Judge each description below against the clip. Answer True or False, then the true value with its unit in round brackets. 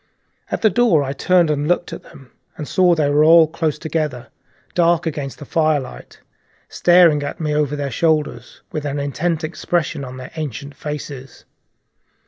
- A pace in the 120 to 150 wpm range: False (165 wpm)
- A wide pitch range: False (2.8 semitones)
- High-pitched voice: False (150 Hz)